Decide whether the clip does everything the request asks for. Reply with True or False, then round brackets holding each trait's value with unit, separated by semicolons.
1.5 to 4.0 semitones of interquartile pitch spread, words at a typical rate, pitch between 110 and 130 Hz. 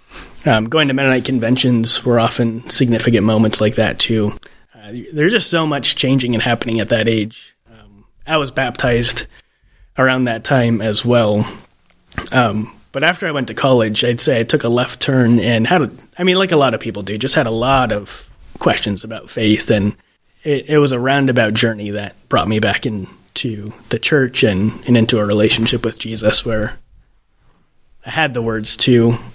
True (3.1 semitones; 185 wpm; 115 Hz)